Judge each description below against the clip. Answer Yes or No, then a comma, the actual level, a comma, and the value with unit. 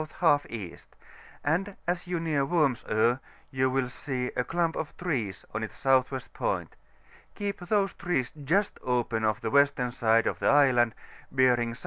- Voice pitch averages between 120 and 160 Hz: Yes, low, 135 Hz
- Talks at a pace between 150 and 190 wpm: Yes, average, 165 wpm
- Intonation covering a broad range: Yes, wide, 5.7 semitones